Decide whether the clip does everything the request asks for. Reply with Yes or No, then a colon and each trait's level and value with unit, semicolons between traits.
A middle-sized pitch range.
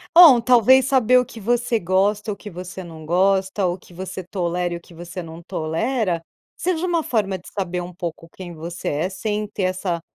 Yes: average, 4.3 semitones